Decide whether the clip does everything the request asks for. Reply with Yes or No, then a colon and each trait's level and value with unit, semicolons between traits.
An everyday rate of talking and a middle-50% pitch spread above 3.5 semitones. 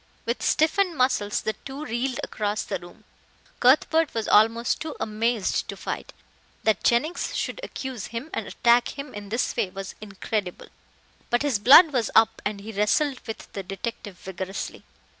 Yes: average, 160 wpm; average, 4.3 semitones